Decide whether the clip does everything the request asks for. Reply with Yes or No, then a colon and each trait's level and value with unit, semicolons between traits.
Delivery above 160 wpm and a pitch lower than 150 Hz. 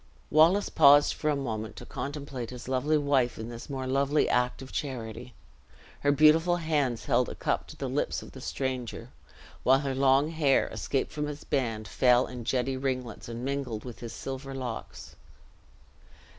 Yes: average, 170 wpm; low, 135 Hz